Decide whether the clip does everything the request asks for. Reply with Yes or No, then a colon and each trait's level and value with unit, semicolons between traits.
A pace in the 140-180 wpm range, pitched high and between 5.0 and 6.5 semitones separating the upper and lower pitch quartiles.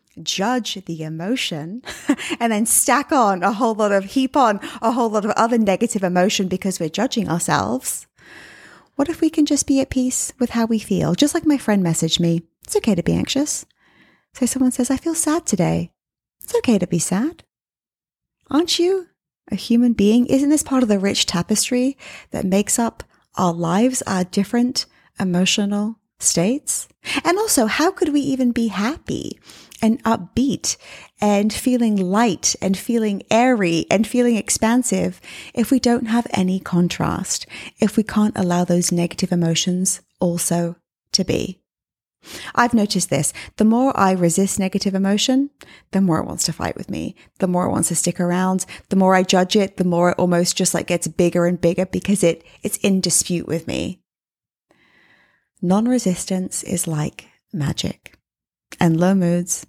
Yes: average, 170 wpm; high, 205 Hz; wide, 5.6 semitones